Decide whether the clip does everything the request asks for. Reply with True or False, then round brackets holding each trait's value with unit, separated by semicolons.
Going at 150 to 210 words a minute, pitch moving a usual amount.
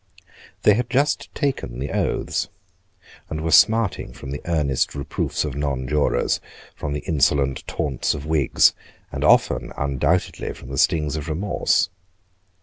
False (140 wpm; 3.5 semitones)